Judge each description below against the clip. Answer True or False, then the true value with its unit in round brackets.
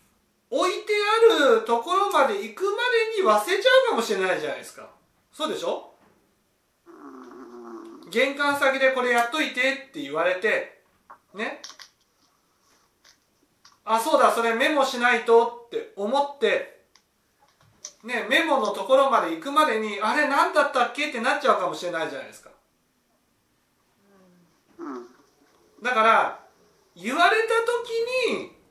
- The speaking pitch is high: True (285 Hz)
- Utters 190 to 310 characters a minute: True (265 characters per minute)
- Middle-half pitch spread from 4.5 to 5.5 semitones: False (8.9 semitones)